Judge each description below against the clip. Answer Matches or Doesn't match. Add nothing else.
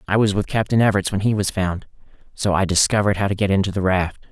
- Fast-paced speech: Matches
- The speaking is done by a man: Matches